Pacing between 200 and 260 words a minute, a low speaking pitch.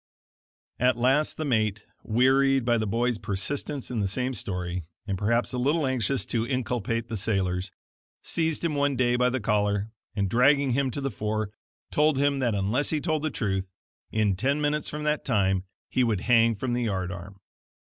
No: average, 185 wpm; low, 120 Hz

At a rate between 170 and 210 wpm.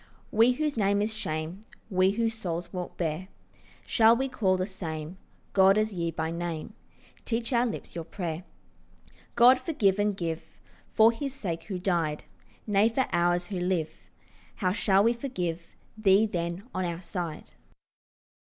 No: average, 155 wpm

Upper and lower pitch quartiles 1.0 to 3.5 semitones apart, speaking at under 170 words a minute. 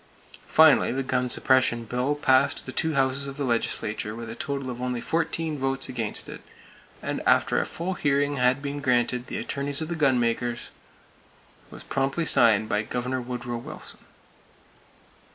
Yes: average, 2.7 semitones; average, 160 wpm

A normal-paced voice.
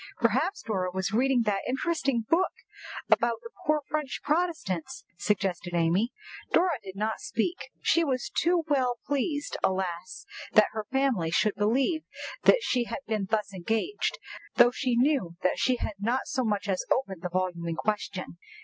Yes: average, 160 wpm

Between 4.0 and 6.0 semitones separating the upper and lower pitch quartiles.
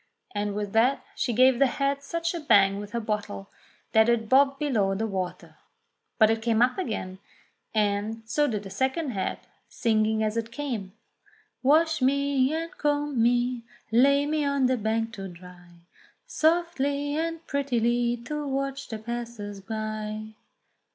Yes: average, 4.7 semitones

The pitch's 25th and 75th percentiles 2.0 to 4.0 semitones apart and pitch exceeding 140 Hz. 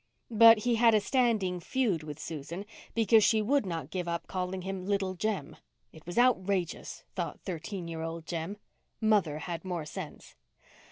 No: average, 4.5 semitones; medium, 185 Hz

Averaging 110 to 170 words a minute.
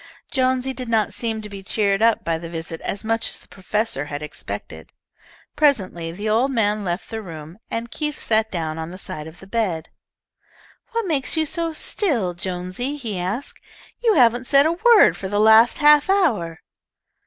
No: average, 185 wpm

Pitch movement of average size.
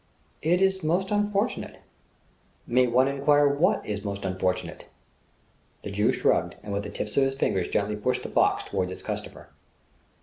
No: wide, 7.7 semitones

